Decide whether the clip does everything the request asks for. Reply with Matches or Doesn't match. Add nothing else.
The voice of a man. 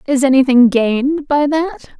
Doesn't match